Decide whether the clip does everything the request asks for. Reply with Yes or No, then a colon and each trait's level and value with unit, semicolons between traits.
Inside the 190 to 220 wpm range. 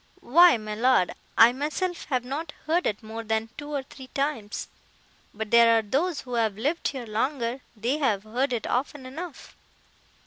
No: average, 175 wpm